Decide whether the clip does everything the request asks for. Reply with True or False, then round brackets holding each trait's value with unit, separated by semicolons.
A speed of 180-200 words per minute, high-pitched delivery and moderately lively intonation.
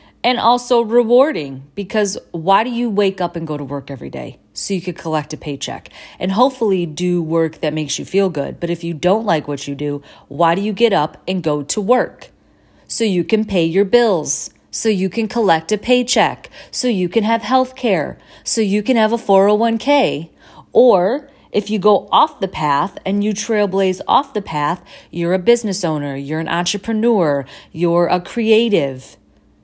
False (190 wpm; 195 Hz; 5.7 semitones)